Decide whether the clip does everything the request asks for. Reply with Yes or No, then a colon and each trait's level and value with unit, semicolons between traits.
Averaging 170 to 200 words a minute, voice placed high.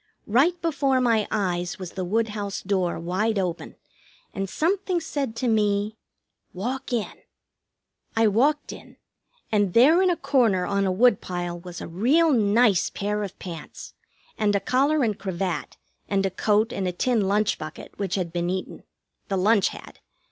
No: average, 160 wpm; high, 205 Hz